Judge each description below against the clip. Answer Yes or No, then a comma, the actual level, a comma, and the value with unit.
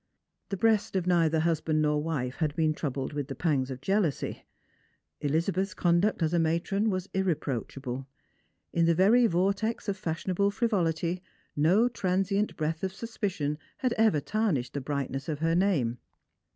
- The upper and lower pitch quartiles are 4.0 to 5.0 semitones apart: Yes, average, 4.7 semitones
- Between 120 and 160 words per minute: Yes, average, 150 wpm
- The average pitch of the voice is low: No, medium, 170 Hz